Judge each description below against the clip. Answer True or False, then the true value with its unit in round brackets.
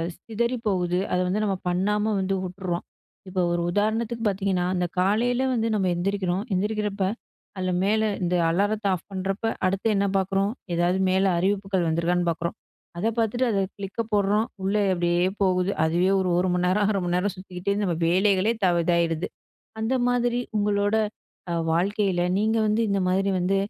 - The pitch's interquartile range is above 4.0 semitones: False (2.5 semitones)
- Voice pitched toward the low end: False (195 Hz)